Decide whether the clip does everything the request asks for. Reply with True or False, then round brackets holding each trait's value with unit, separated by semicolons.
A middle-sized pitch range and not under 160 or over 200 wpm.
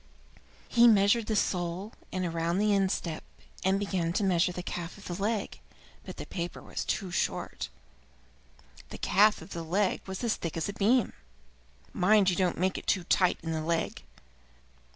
True (3.0 semitones; 175 wpm)